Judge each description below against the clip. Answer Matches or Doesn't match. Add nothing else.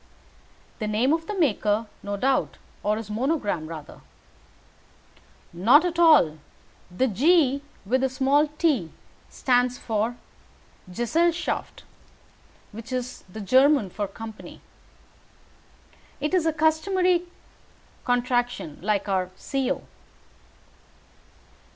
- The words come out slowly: Matches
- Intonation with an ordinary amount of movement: Doesn't match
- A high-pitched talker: Matches